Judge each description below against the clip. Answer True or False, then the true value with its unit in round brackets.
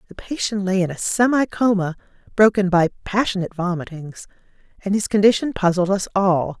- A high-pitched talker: True (195 Hz)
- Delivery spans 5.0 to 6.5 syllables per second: True (5.6 syllables/s)